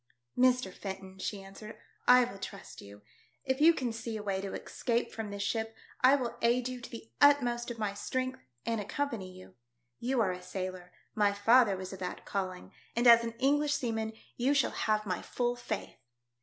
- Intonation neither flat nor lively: Yes, average, 4.2 semitones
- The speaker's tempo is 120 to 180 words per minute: No, average, 200 wpm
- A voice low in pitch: No, high, 225 Hz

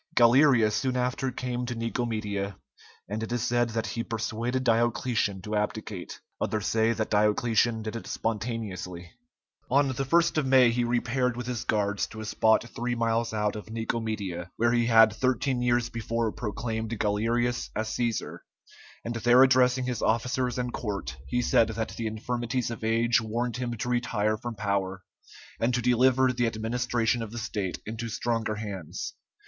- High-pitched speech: No, low, 115 Hz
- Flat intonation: Yes, narrow, 2.0 semitones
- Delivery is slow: No, average, 165 wpm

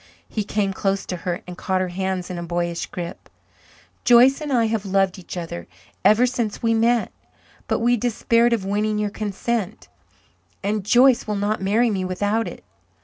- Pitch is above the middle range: Yes, high, 205 Hz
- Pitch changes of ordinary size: Yes, average, 3.5 semitones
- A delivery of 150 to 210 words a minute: Yes, average, 180 wpm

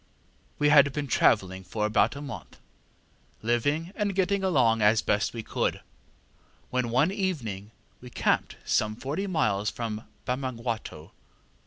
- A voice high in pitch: No, low, 120 Hz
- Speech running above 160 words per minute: No, slow, 135 wpm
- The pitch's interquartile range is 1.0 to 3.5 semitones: No, wide, 5.5 semitones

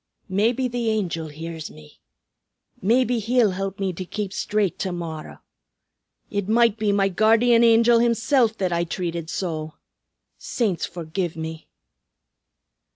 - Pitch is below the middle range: No, high, 195 Hz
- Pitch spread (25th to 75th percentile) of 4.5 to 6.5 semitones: Yes, average, 5.0 semitones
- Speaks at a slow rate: Yes, slow, 130 wpm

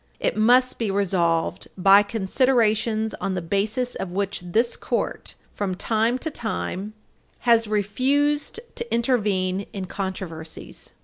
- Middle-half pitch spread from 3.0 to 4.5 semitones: Yes, average, 3.7 semitones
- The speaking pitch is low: No, high, 210 Hz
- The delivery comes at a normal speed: No, slow, 125 wpm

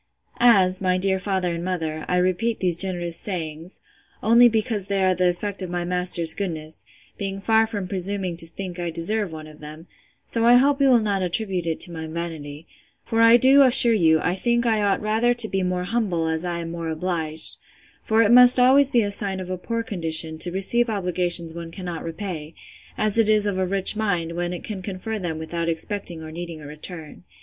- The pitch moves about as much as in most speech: Yes, average, 4.2 semitones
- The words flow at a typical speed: No, fast, 210 wpm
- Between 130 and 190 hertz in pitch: Yes, medium, 185 Hz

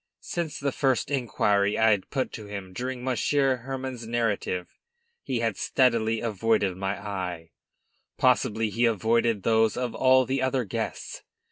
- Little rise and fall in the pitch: No, average, 4.0 semitones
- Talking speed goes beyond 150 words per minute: No, average, 145 wpm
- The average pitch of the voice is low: Yes, low, 115 Hz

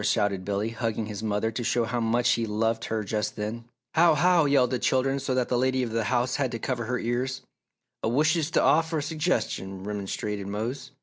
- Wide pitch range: No, average, 3.5 semitones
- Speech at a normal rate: No, fast, 210 wpm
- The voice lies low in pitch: Yes, low, 120 Hz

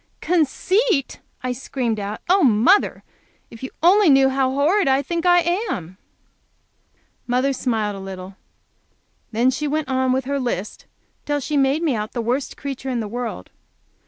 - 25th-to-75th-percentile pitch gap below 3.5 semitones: No, average, 4.1 semitones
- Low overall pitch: No, very high, 265 Hz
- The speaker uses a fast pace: No, average, 160 wpm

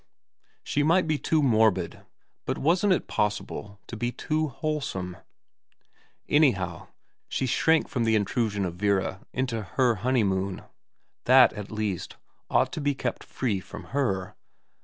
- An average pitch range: No, wide, 6.1 semitones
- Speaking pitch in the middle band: No, low, 115 Hz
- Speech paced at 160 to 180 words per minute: No, slow, 135 wpm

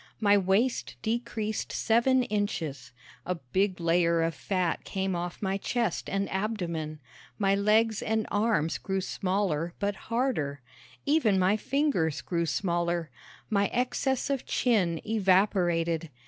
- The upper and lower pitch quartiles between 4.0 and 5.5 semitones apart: Yes, average, 4.4 semitones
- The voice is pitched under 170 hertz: No, high, 195 Hz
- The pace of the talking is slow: Yes, slow, 125 wpm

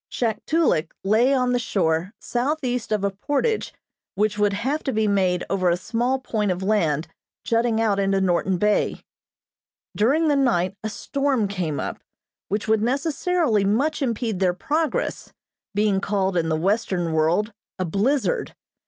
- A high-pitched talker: Yes, high, 210 Hz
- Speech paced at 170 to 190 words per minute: No, average, 155 wpm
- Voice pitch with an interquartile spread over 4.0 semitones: Yes, average, 4.8 semitones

